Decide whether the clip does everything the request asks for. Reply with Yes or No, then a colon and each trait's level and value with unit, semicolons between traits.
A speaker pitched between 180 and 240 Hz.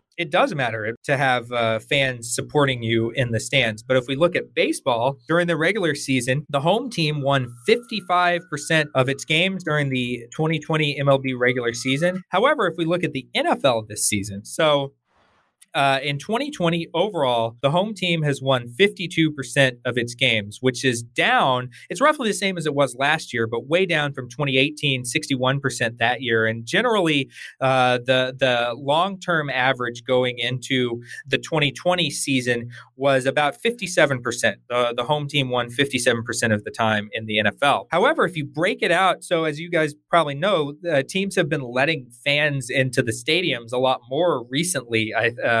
No: low, 135 Hz